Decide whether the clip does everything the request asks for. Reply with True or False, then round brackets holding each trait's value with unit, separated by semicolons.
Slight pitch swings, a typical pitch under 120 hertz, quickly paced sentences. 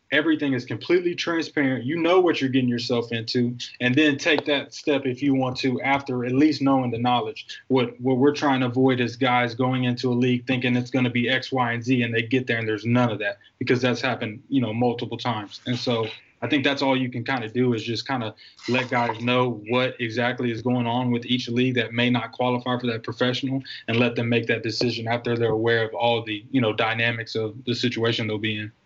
False (1.9 semitones; 125 Hz; 245 wpm)